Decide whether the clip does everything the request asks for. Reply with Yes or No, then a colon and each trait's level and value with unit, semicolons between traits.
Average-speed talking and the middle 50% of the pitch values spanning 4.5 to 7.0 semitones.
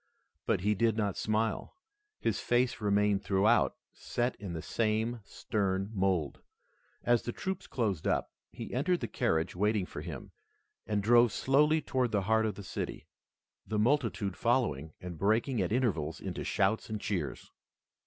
No: average, 155 wpm; average, 3.7 semitones